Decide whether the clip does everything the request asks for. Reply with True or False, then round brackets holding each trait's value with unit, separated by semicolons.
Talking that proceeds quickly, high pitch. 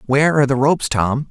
False (230 wpm; 135 Hz)